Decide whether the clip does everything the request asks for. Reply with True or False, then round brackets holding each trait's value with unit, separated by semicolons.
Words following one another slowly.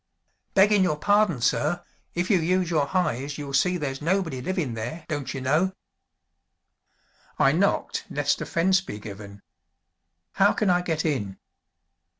False (145 wpm)